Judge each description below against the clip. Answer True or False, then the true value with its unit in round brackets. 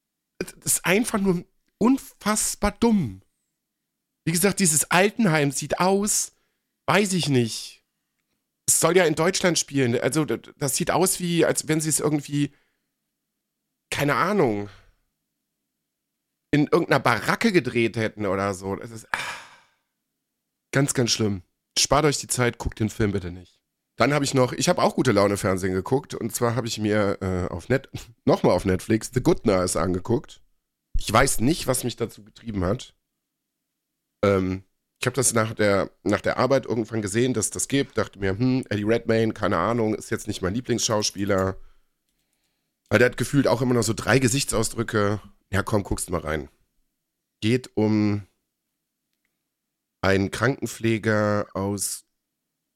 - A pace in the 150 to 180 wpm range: True (155 wpm)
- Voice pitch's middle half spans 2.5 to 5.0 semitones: False (5.6 semitones)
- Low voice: True (115 Hz)